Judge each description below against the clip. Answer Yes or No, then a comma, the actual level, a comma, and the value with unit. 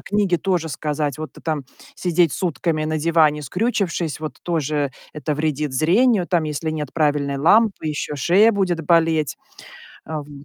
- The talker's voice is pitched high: No, medium, 155 Hz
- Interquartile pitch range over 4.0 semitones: No, average, 2.8 semitones